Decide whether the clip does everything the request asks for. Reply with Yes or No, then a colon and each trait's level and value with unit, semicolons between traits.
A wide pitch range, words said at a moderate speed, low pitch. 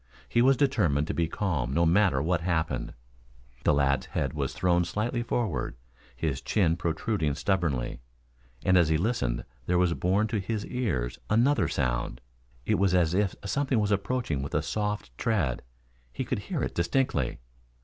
Yes: wide, 6.5 semitones; average, 165 wpm; very low, 85 Hz